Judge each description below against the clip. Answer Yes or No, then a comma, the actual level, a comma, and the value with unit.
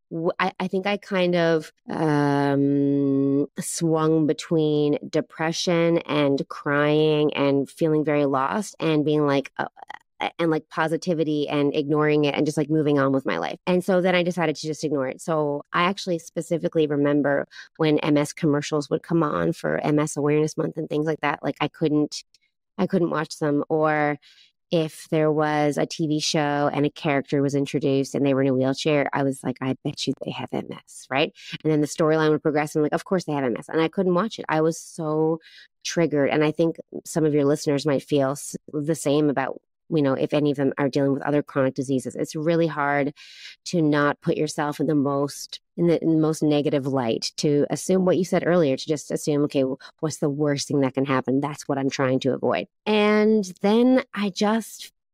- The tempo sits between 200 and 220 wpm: Yes, fast, 205 wpm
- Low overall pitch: No, medium, 150 Hz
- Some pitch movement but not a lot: No, narrow, 2.3 semitones